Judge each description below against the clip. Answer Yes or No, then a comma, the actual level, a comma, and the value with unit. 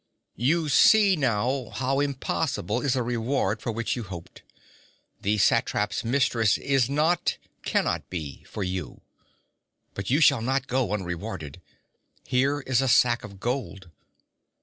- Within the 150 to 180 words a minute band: No, slow, 135 wpm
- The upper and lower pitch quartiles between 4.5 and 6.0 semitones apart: Yes, average, 4.8 semitones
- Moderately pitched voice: No, low, 120 Hz